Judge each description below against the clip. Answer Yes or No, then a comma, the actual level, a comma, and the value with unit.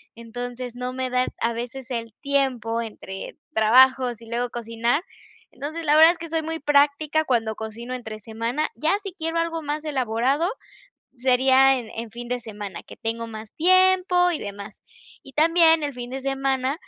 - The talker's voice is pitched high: Yes, very high, 255 Hz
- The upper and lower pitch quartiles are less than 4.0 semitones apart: No, average, 4.8 semitones